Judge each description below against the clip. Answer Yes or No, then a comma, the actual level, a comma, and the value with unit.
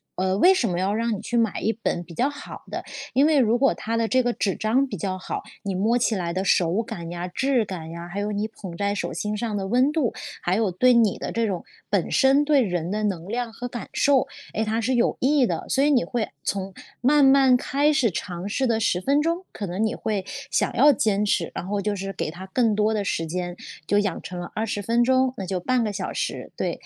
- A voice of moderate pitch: No, high, 215 Hz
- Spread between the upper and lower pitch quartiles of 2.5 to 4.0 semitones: No, average, 4.8 semitones